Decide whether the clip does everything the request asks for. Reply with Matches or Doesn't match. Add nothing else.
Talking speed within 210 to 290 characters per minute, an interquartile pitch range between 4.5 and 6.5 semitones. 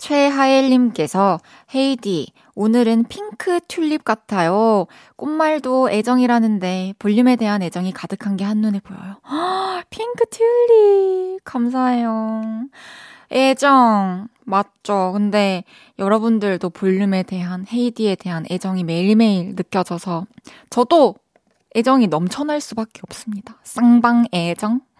Matches